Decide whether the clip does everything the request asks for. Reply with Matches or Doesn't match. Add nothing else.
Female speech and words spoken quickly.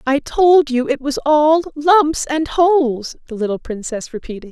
Doesn't match